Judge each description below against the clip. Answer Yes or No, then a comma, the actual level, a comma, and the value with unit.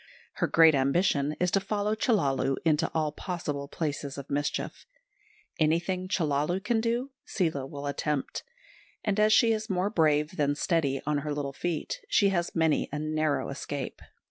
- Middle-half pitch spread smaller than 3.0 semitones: No, average, 4.5 semitones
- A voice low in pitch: No, medium, 155 Hz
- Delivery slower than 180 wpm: Yes, average, 160 wpm